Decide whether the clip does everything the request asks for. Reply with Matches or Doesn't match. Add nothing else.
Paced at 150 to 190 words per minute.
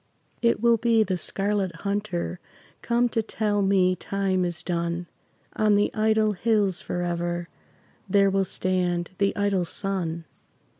Doesn't match